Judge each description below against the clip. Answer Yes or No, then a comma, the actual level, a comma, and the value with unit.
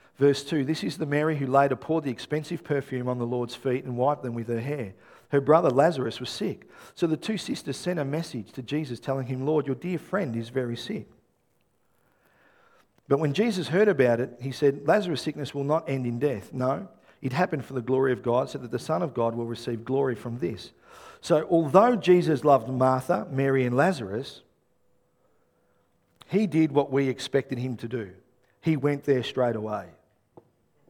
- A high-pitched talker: No, low, 135 Hz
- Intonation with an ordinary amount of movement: Yes, average, 3.9 semitones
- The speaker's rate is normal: Yes, average, 195 wpm